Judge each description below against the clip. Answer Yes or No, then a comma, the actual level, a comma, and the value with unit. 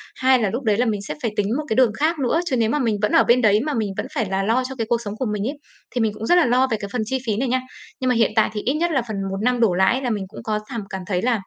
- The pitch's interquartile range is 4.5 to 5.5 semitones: No, average, 3.4 semitones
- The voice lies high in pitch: Yes, high, 230 Hz